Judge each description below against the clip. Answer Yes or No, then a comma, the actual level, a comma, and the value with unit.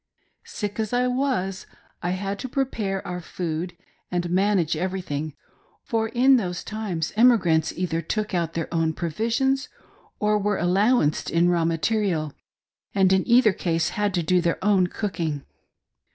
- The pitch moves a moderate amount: Yes, average, 4.3 semitones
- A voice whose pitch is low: No, medium, 185 Hz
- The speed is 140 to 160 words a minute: Yes, average, 150 wpm